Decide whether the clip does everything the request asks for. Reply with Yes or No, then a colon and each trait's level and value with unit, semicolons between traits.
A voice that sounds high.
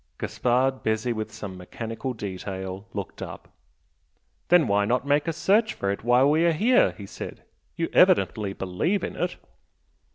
No: low, 120 Hz